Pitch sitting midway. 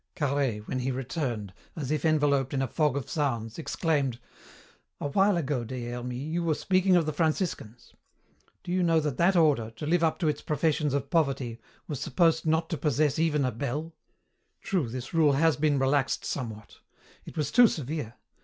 Yes: medium, 145 Hz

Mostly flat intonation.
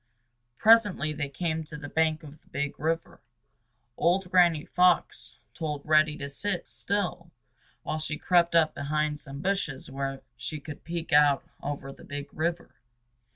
No: average, 3.0 semitones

